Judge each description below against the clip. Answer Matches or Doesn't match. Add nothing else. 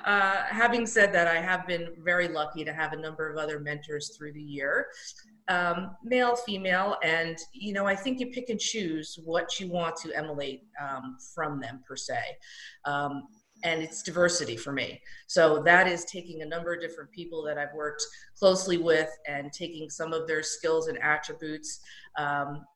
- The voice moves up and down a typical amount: Matches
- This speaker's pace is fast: Doesn't match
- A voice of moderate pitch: Matches